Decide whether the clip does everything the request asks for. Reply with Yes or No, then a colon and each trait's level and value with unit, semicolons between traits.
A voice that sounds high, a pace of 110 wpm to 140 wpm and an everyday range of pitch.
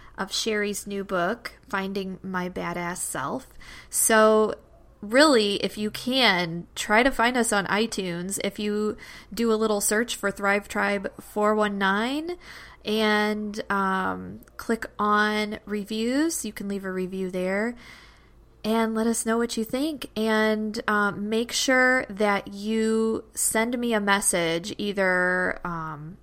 No: high, 210 Hz; slow, 135 wpm; narrow, 2.2 semitones